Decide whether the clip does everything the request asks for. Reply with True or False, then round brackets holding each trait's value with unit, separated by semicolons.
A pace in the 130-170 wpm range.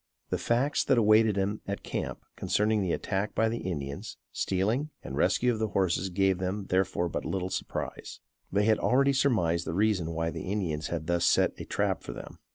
False (195 wpm)